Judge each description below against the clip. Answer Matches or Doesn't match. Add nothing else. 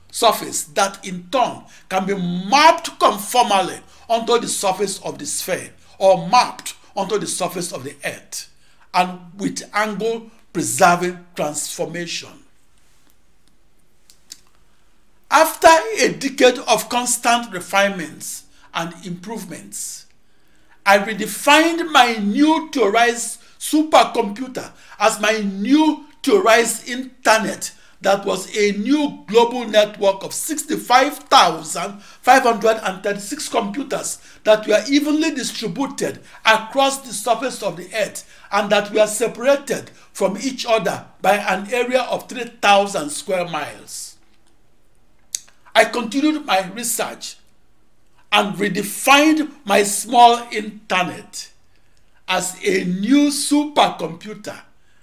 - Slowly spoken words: Matches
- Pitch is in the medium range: Doesn't match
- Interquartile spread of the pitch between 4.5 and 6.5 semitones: Matches